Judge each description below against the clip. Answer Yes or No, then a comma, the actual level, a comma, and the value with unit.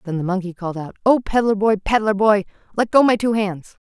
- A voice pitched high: Yes, high, 205 Hz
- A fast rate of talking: Yes, fast, 235 wpm